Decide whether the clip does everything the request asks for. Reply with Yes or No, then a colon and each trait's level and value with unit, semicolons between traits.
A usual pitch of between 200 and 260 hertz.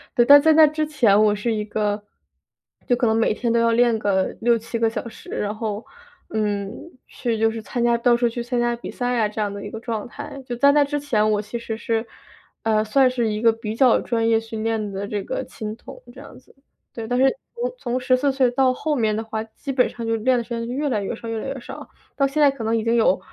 Yes: high, 230 Hz